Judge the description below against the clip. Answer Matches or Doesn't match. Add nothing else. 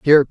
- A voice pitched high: Doesn't match